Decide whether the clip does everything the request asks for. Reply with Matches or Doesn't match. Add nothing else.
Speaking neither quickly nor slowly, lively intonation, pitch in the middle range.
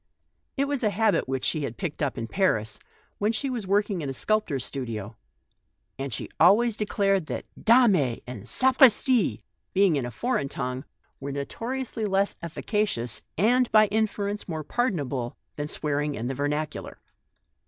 Matches